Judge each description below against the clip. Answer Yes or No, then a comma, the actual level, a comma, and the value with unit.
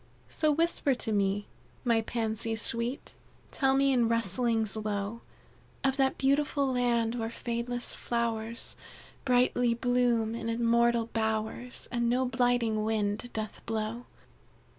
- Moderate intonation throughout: No, narrow, 1.9 semitones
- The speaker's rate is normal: No, slow, 120 wpm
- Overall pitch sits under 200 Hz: No, high, 235 Hz